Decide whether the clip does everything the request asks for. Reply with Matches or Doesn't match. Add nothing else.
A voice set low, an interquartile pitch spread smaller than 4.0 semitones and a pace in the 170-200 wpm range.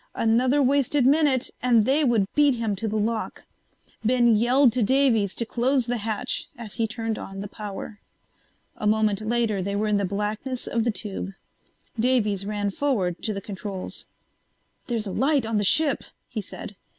Doesn't match